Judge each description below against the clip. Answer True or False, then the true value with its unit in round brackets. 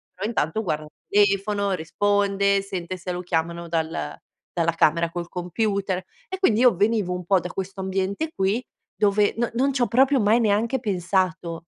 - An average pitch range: True (3.2 semitones)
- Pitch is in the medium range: False (195 Hz)